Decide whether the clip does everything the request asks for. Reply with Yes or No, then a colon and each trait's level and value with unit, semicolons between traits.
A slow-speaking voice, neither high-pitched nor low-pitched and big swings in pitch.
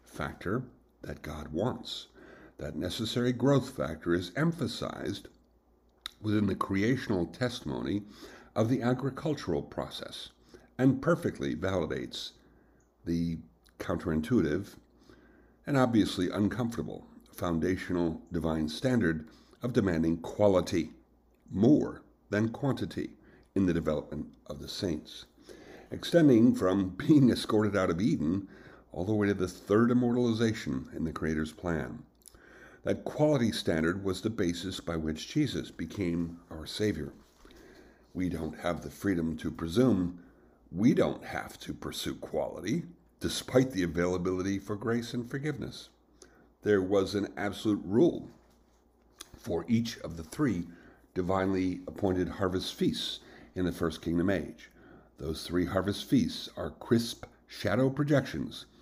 No: slow, 120 wpm; very low, 95 Hz; wide, 5.7 semitones